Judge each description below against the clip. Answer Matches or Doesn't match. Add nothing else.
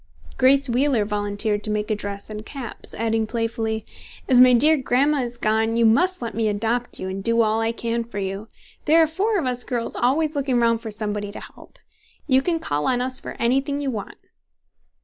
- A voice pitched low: Doesn't match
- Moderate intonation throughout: Matches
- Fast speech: Matches